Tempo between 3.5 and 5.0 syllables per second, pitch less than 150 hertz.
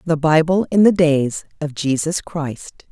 No: 4.1 syllables/s; medium, 160 Hz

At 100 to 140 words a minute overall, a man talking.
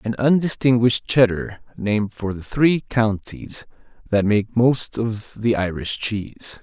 Yes: slow, 135 wpm; male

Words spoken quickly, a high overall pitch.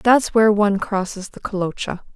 No: average, 165 wpm; high, 205 Hz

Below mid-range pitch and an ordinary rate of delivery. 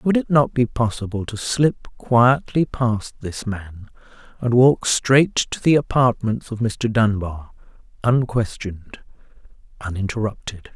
No: low, 115 Hz; slow, 125 wpm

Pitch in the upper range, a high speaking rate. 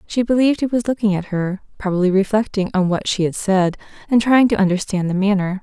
Yes: high, 200 Hz; fast, 215 wpm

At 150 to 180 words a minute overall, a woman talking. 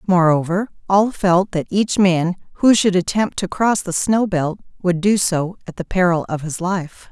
No: average, 195 wpm; female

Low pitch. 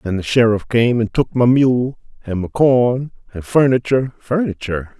Yes: low, 120 Hz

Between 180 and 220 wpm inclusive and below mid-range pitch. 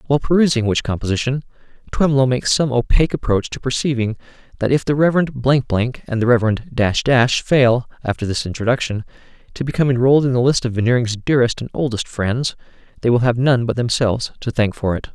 Yes: average, 190 wpm; low, 125 Hz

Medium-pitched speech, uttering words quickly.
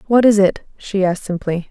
No: high, 195 Hz; fast, 210 wpm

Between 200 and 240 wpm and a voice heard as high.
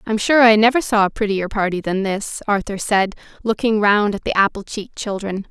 Yes: fast, 205 wpm; high, 210 Hz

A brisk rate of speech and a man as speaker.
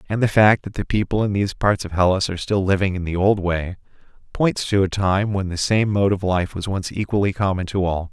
Yes: fast, 250 wpm; male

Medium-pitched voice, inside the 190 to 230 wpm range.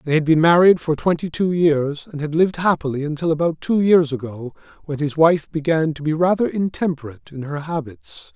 Yes: medium, 160 Hz; average, 200 wpm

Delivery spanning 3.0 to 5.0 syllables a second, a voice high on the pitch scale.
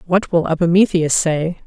No: 4.7 syllables/s; medium, 170 Hz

